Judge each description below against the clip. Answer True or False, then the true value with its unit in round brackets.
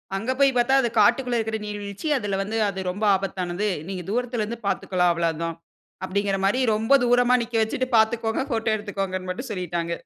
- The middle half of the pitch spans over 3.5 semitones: True (3.9 semitones)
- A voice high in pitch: True (210 Hz)